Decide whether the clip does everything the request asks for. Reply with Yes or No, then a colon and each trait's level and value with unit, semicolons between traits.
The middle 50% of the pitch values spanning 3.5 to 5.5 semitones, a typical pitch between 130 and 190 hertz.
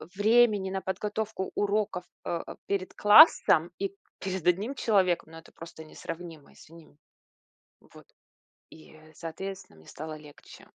Yes: average, 4.0 semitones; medium, 185 Hz